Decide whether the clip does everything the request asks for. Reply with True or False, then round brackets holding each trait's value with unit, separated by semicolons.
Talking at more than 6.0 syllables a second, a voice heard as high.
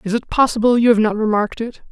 True (6.8 syllables/s; 225 Hz)